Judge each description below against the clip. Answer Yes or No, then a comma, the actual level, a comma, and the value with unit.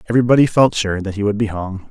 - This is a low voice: Yes, low, 105 Hz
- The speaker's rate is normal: No, fast, 250 wpm